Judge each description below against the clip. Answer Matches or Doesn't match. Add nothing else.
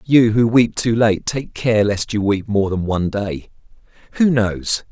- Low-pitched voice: Matches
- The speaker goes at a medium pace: Matches